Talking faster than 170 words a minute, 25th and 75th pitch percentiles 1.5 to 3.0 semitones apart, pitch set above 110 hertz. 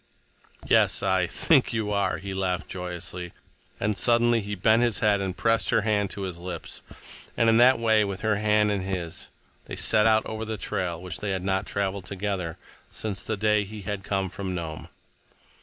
No: average, 190 wpm; narrow, 2.6 semitones; low, 100 Hz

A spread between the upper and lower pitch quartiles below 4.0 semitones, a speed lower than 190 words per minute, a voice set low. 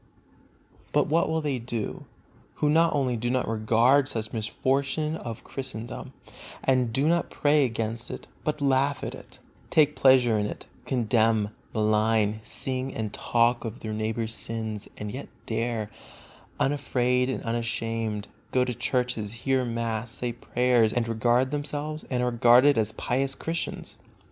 Yes: average, 3.1 semitones; average, 150 wpm; low, 120 Hz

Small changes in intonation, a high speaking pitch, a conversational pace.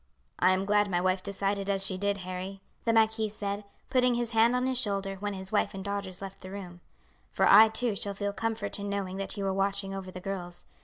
No: narrow, 1.6 semitones; high, 200 Hz; fast, 235 wpm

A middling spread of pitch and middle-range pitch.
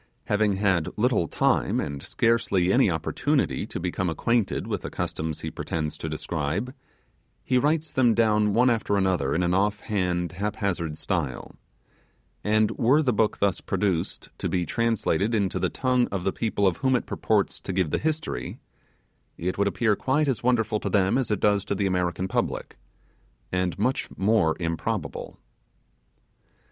No: average, 4.3 semitones; low, 100 Hz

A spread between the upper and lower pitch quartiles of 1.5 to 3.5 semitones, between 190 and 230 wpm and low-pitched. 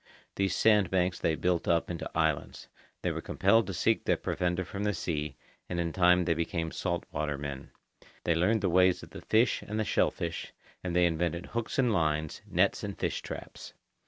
Yes: average, 3.0 semitones; average, 195 wpm; very low, 90 Hz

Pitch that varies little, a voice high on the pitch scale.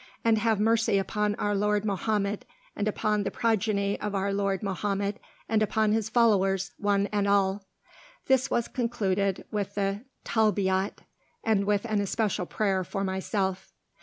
Yes: narrow, 1.6 semitones; high, 205 Hz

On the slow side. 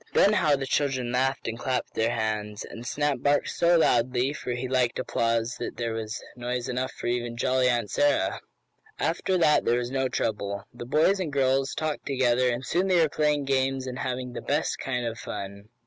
No: average, 200 wpm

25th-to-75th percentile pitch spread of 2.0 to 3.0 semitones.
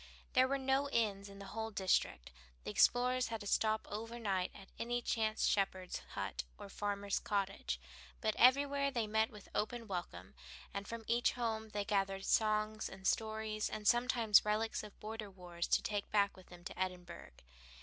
Yes: narrow, 2.6 semitones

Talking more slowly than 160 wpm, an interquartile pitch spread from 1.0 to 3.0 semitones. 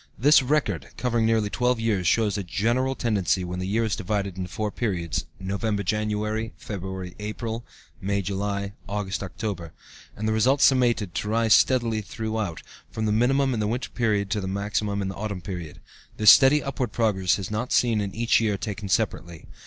No: average, 185 wpm; average, 2.7 semitones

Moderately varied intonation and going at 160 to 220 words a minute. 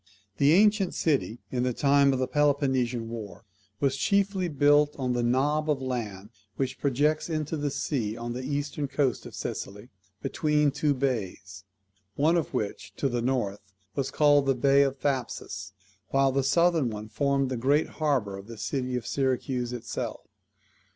Yes: average, 3.2 semitones; average, 165 wpm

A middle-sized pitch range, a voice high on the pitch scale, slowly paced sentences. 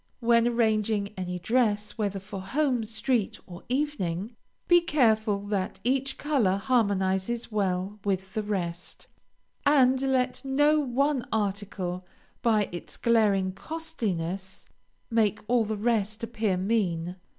Yes: average, 4.4 semitones; high, 215 Hz; slow, 120 wpm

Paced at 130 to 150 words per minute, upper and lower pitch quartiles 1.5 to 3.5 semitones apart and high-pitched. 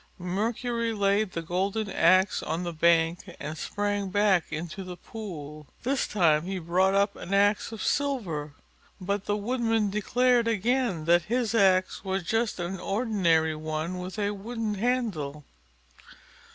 No: average, 145 wpm; average, 4.3 semitones; high, 195 Hz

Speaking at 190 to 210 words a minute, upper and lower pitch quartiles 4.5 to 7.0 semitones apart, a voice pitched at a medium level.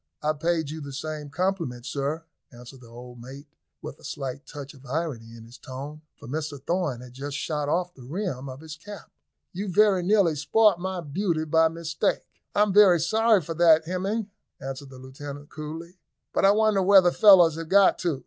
Yes: average, 195 wpm; average, 4.9 semitones; medium, 160 Hz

